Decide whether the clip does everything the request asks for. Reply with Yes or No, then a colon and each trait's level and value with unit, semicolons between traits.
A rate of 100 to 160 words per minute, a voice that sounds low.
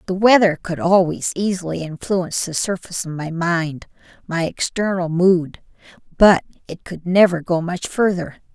No: average, 150 wpm; medium, 175 Hz